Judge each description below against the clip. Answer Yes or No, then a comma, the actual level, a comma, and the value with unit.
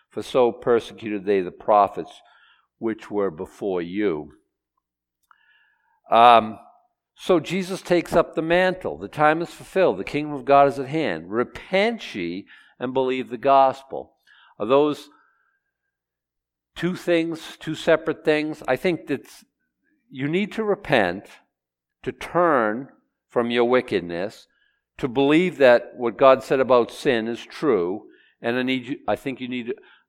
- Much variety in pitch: Yes, wide, 6.3 semitones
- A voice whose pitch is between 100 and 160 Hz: Yes, medium, 140 Hz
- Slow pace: No, average, 145 wpm